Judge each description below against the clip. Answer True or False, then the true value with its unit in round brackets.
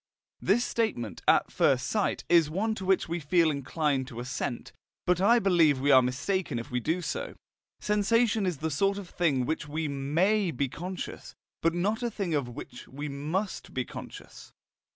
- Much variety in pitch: True (5.7 semitones)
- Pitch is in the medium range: True (165 Hz)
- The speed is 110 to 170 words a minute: False (185 wpm)